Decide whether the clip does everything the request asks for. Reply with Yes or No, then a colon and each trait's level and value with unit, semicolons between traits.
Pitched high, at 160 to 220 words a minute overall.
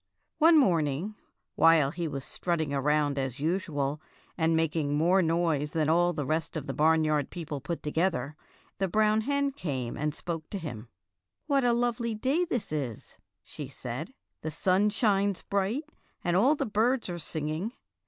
No: medium, 165 Hz; average, 165 wpm